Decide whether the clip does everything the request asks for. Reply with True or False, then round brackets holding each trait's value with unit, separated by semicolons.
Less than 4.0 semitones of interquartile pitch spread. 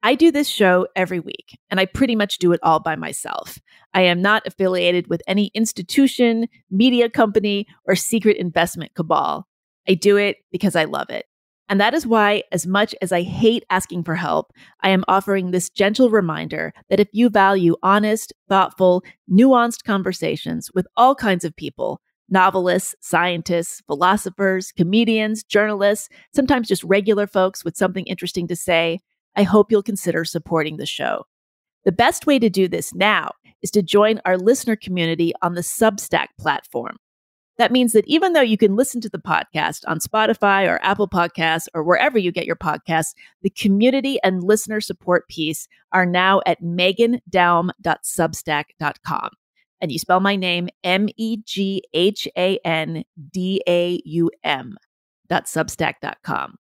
True (3.4 semitones)